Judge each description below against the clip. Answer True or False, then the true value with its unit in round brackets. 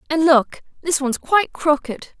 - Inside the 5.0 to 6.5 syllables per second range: True (5.7 syllables/s)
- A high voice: True (300 Hz)